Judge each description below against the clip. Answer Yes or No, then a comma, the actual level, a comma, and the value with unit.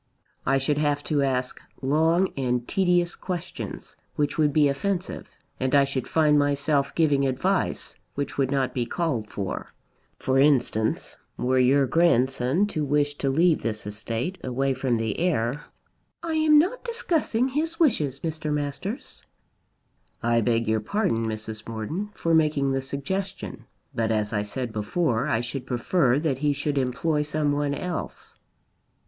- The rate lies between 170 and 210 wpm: No, average, 155 wpm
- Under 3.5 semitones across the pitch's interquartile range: No, average, 4.6 semitones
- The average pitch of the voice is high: No, medium, 140 Hz